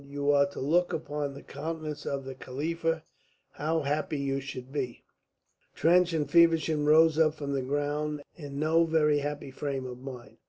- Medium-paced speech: Yes, average, 170 wpm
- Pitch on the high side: No, medium, 145 Hz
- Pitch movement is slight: Yes, narrow, 2.3 semitones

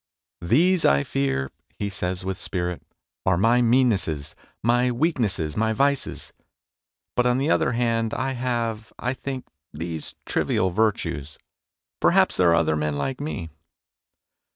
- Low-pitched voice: Yes, low, 110 Hz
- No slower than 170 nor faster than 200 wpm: No, average, 145 wpm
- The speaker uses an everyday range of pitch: No, wide, 6.7 semitones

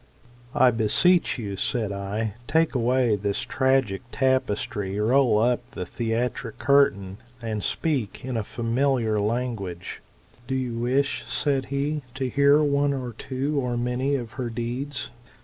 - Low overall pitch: Yes, low, 125 Hz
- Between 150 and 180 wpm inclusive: No, slow, 135 wpm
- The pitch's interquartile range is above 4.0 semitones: No, average, 3.6 semitones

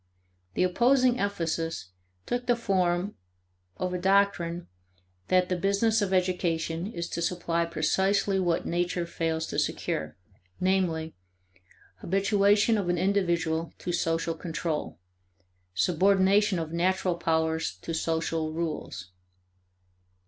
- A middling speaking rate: No, slow, 110 wpm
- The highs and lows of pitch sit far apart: No, average, 3.1 semitones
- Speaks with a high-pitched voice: No, medium, 175 Hz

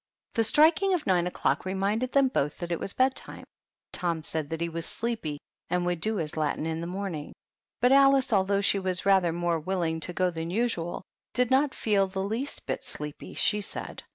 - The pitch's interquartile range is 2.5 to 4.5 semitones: No, average, 5.2 semitones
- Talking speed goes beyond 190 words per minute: Yes, average, 200 wpm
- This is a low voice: No, high, 190 Hz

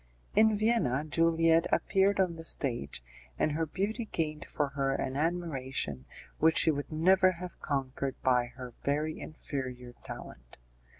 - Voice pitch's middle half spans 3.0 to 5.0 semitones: Yes, average, 4.5 semitones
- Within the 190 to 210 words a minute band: No, average, 140 wpm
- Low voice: No, medium, 155 Hz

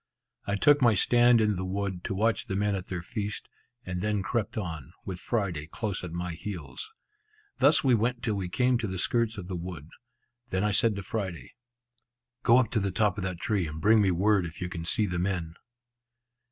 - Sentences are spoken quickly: Yes, fast, 215 wpm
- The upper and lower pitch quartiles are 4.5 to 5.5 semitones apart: No, average, 3.7 semitones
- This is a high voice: No, low, 100 Hz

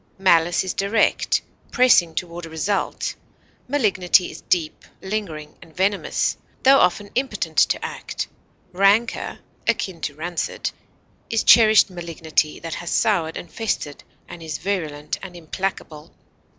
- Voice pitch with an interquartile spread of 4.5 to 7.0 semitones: No, average, 3.8 semitones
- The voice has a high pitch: No, medium, 180 Hz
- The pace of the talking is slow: Yes, slow, 125 wpm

